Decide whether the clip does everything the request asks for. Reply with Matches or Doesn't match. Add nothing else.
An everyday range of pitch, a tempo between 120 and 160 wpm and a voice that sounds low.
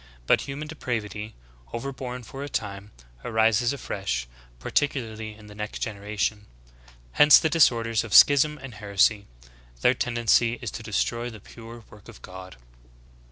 Matches